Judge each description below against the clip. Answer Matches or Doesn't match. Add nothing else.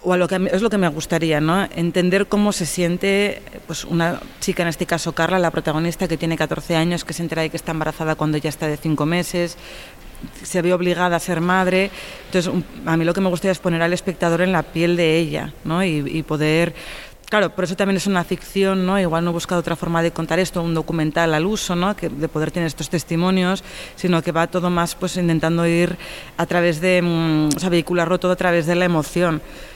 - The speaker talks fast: Matches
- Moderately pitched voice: Matches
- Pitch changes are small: Matches